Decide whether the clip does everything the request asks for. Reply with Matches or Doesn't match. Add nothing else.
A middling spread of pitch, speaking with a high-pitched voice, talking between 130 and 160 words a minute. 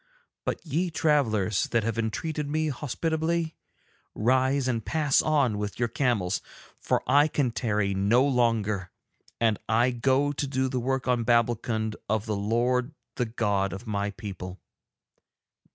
Doesn't match